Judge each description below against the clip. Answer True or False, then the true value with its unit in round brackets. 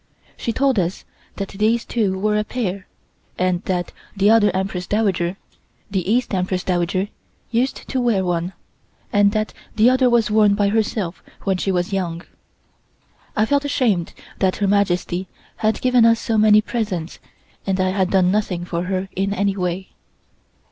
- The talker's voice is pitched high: True (195 Hz)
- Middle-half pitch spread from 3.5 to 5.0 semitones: False (2.9 semitones)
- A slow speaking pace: False (165 wpm)